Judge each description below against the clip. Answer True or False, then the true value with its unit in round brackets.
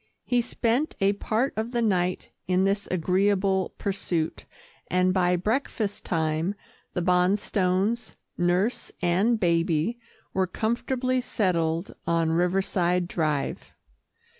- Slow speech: True (110 wpm)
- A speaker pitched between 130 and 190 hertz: True (185 Hz)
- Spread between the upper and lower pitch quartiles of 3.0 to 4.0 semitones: True (3.6 semitones)